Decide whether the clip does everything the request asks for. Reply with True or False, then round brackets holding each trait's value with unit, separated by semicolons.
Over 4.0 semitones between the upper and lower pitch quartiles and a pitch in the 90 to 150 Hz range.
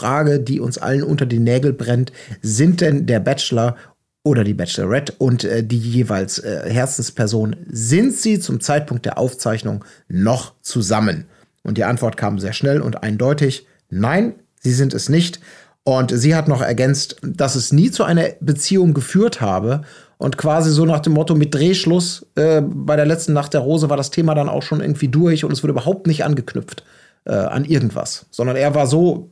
True (4.5 semitones; 140 Hz)